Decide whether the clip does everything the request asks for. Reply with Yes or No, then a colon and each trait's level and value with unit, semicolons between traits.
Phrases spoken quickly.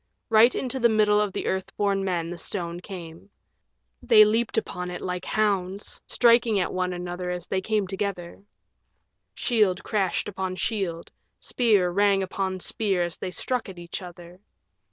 No: average, 160 wpm